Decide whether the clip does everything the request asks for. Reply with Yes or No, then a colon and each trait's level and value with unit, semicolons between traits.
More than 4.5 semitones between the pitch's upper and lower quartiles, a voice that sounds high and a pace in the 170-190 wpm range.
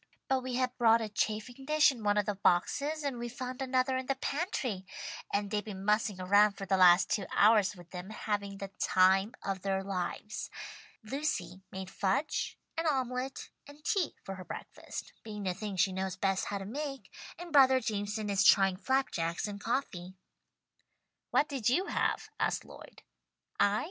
Yes: average, 5.2 semitones; high, 210 Hz; average, 180 wpm